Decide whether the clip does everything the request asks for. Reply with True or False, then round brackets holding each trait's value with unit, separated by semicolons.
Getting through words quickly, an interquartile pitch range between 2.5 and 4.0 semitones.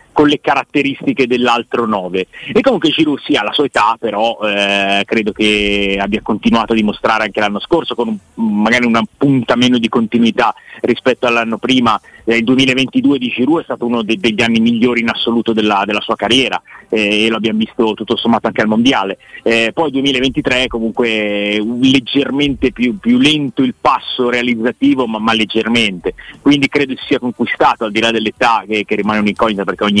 True (190 wpm; 3.3 semitones)